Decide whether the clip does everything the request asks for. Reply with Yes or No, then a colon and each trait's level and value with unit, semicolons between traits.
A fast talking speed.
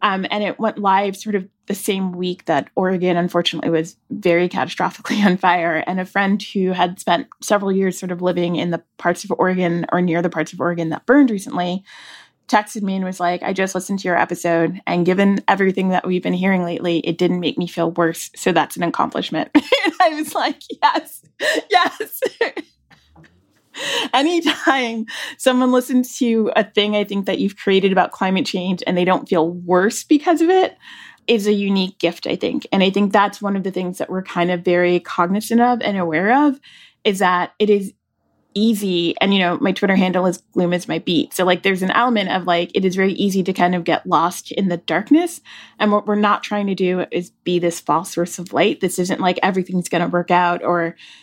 Yes: fast, 210 wpm